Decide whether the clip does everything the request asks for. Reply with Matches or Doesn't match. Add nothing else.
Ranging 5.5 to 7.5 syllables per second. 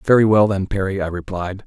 Matches